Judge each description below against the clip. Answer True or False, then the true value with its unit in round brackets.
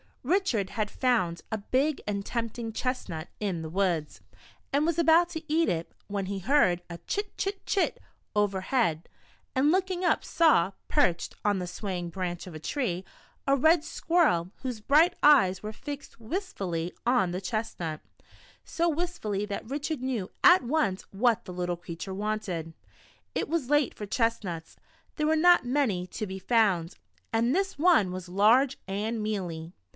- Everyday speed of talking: True (165 wpm)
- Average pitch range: False (8.0 semitones)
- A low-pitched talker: False (220 Hz)